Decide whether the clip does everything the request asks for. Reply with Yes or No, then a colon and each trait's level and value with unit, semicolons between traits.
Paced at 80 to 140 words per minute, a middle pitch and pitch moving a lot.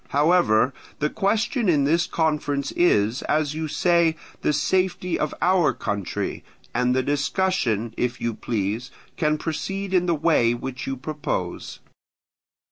Yes: slow, 135 wpm; medium, 150 Hz; wide, 5.7 semitones